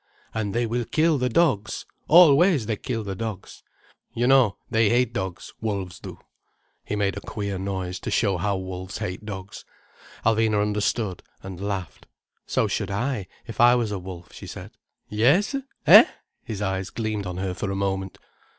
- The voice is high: No, low, 105 Hz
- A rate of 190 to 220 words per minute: No, average, 170 wpm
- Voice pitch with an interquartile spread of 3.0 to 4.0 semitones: Yes, average, 3.6 semitones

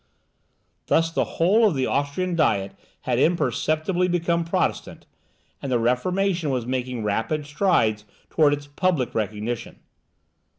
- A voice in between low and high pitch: Yes, medium, 145 Hz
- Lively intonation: Yes, wide, 5.8 semitones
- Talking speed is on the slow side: Yes, slow, 125 wpm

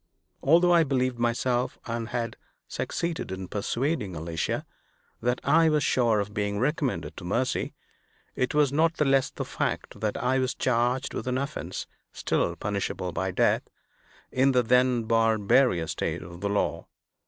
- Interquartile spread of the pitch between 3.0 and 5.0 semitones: Yes, average, 4.7 semitones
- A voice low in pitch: Yes, low, 125 Hz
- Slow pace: No, average, 155 wpm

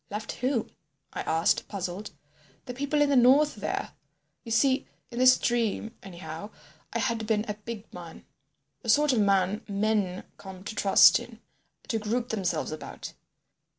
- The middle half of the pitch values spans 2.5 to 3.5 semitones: No, average, 3.9 semitones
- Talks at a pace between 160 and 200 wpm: No, average, 150 wpm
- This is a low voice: No, high, 215 Hz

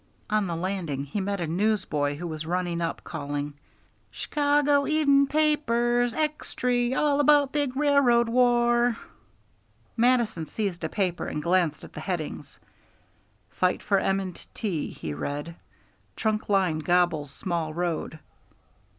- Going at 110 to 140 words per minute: Yes, slow, 135 wpm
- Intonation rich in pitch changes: Yes, wide, 6.8 semitones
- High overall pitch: Yes, high, 200 Hz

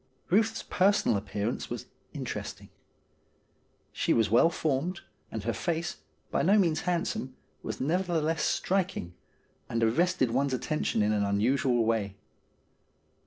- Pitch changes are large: Yes, wide, 7.6 semitones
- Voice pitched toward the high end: No, medium, 140 Hz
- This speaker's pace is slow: Yes, slow, 125 wpm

